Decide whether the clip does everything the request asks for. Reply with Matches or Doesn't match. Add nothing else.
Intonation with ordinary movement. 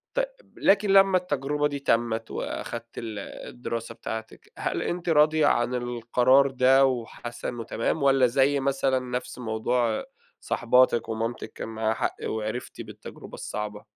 Matches